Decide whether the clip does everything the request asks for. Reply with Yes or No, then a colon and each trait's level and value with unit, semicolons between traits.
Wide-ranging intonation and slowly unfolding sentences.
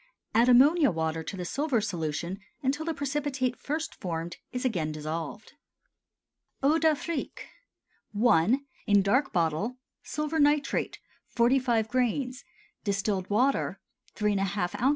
Yes: wide, 7.1 semitones; slow, 115 wpm